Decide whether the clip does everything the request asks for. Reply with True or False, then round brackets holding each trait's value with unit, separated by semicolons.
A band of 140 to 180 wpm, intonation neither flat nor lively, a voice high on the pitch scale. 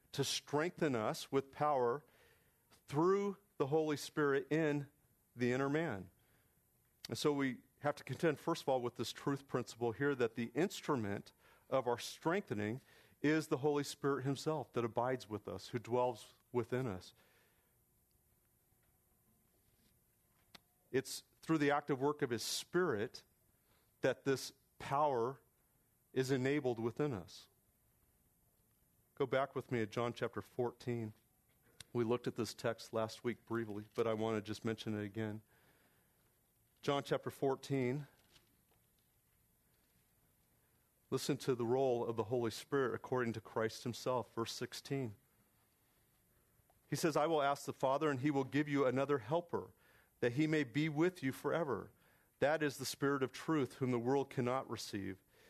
False (145 wpm; 3.7 semitones; 130 Hz)